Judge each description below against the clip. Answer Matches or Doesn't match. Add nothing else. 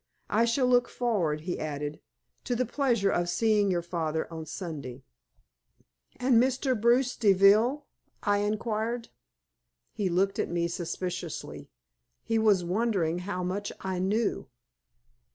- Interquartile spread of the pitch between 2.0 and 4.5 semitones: Doesn't match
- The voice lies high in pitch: Matches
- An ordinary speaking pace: Doesn't match